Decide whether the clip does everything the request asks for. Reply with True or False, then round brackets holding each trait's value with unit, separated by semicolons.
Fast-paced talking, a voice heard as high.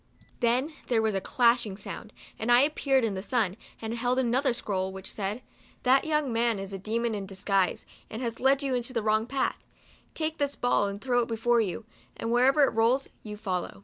True (210 wpm; 235 Hz)